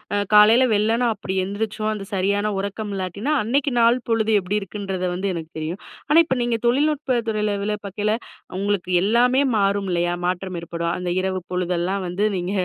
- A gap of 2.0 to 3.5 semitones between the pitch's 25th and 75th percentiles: Yes, average, 3.2 semitones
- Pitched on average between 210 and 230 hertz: No, high, 200 Hz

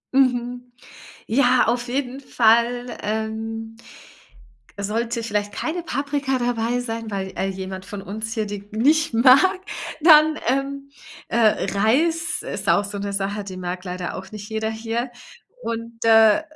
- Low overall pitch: No, high, 230 Hz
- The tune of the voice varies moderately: Yes, average, 3.5 semitones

